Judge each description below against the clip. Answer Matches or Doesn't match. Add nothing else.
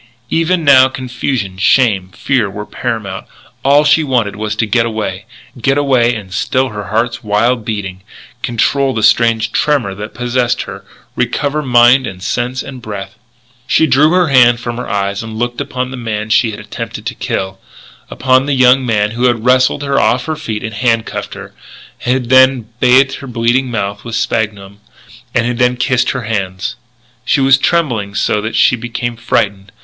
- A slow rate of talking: Doesn't match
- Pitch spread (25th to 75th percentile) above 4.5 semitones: Doesn't match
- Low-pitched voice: Matches